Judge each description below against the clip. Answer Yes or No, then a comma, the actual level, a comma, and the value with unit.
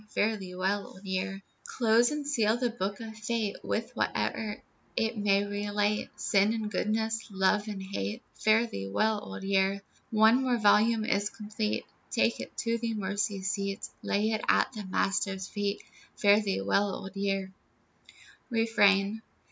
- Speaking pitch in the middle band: No, high, 205 Hz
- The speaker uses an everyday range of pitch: No, narrow, 2.1 semitones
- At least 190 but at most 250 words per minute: No, average, 155 wpm